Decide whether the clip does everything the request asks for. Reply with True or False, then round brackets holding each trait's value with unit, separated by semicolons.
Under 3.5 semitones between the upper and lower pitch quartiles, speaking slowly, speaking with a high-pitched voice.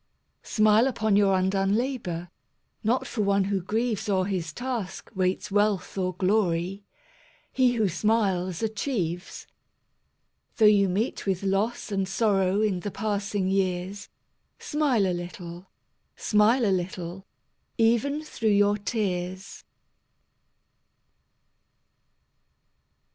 True (2.7 semitones; 110 wpm; 200 Hz)